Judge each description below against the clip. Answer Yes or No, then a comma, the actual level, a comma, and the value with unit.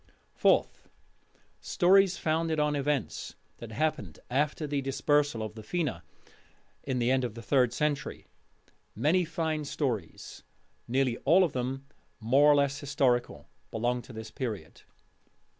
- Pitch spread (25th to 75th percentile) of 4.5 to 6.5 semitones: No, average, 4.0 semitones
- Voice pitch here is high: No, low, 135 Hz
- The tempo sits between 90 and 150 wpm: Yes, slow, 135 wpm